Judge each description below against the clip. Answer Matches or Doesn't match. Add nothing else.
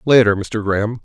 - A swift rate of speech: Doesn't match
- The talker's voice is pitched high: Doesn't match